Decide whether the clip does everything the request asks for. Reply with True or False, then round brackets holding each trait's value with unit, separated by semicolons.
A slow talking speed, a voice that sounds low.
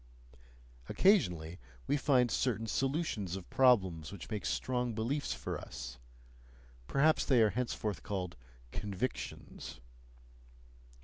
True (105 wpm; 110 Hz)